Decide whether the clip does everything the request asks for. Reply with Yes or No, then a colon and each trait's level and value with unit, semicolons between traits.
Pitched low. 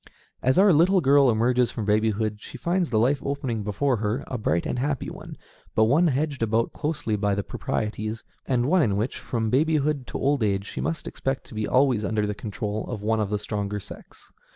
Yes: low, 115 Hz